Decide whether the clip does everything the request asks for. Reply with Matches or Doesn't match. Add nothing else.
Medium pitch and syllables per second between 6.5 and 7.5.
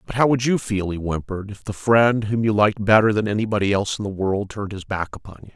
Doesn't match